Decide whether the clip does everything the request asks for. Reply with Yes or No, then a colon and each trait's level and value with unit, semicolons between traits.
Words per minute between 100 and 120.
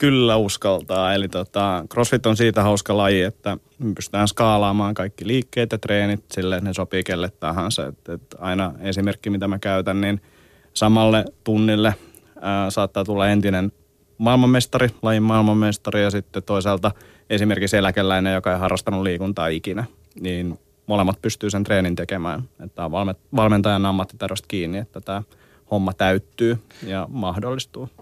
No: average, 145 wpm